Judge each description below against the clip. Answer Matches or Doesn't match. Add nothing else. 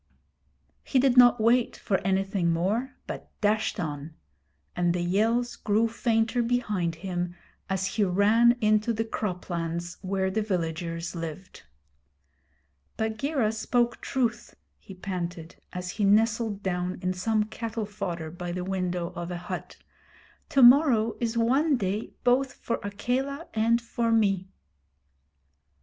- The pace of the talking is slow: Matches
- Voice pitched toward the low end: Doesn't match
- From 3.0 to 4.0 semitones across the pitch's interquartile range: Doesn't match